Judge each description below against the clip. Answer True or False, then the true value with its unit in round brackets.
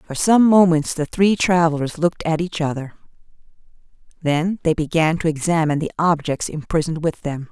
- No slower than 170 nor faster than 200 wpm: False (160 wpm)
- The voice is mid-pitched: True (160 Hz)